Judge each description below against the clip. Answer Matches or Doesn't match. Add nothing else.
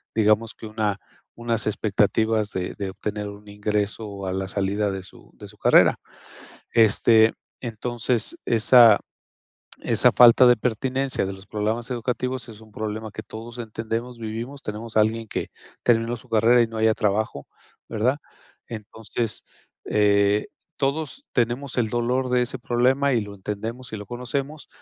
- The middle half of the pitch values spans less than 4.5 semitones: Matches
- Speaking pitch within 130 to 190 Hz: Doesn't match